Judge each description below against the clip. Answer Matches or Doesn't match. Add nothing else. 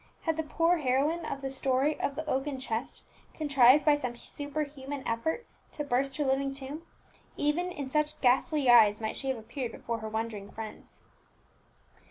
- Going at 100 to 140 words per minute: Doesn't match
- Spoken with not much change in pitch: Doesn't match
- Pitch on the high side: Matches